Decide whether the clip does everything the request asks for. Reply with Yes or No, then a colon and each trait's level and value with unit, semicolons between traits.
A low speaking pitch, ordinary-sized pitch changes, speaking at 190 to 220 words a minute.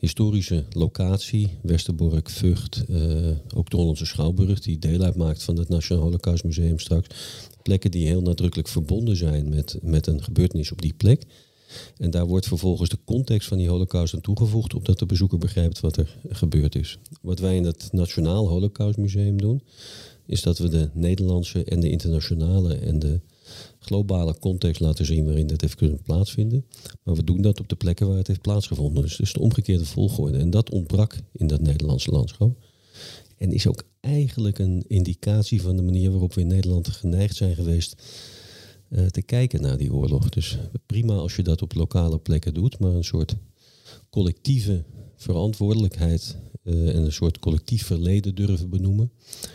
No: very low, 95 Hz; average, 4.1 semitones; average, 175 wpm